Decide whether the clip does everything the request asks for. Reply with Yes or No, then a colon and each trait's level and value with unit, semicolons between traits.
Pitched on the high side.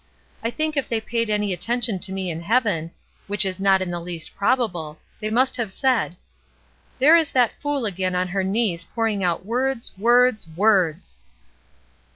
Yes: high, 210 Hz